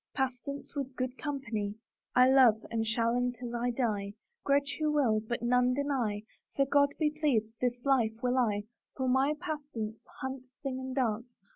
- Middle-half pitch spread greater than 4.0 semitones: No, average, 3.2 semitones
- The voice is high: Yes, very high, 250 Hz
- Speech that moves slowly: No, average, 165 wpm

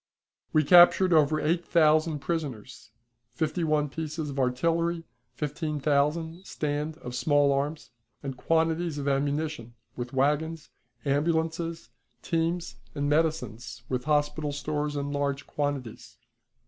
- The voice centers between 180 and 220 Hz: No, medium, 150 Hz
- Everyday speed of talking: No, slow, 120 wpm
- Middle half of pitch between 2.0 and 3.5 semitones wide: Yes, narrow, 2.4 semitones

